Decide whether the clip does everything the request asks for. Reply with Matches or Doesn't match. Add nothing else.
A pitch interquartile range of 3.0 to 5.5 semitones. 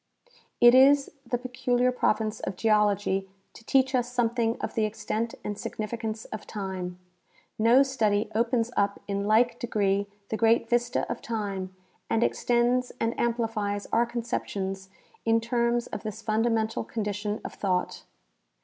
Doesn't match